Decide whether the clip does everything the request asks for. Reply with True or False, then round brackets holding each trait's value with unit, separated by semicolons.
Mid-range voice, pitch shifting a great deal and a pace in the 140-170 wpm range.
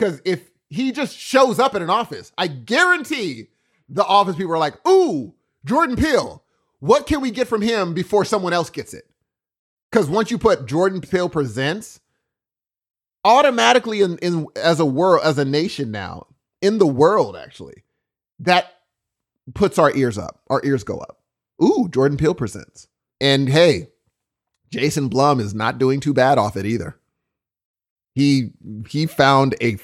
True (160 Hz; 7.3 semitones; 160 wpm)